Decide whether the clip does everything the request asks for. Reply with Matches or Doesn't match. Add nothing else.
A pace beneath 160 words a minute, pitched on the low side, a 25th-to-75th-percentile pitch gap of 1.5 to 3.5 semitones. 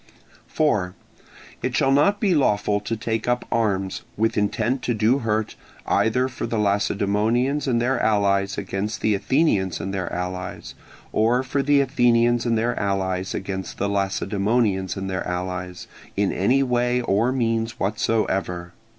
Doesn't match